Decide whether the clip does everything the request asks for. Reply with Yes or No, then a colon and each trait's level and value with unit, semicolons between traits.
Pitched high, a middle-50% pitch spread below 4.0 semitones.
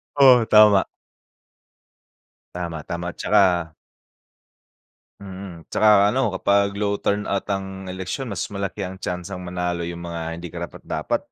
No: very low, 95 Hz; narrow, 2.6 semitones